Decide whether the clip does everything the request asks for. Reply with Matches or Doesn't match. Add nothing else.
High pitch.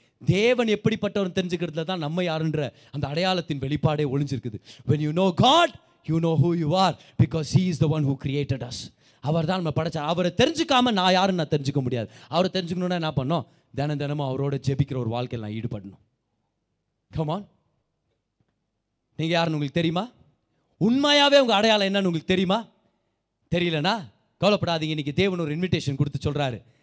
Doesn't match